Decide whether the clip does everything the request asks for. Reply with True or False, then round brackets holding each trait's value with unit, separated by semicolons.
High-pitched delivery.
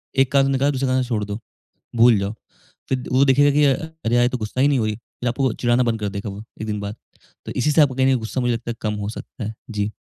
False (120 Hz)